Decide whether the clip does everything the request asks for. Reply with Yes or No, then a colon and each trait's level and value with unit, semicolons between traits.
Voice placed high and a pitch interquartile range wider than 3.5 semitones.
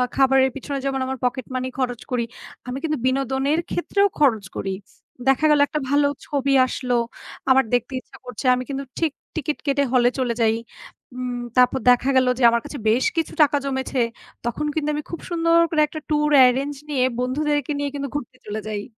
No: very high, 270 Hz; average, 2.8 semitones